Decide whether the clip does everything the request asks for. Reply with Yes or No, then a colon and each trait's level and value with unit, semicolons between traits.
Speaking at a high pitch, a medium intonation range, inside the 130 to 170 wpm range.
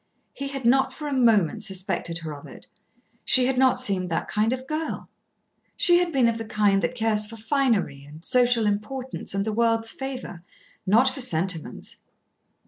No: high, 225 Hz; average, 5.0 semitones; average, 180 wpm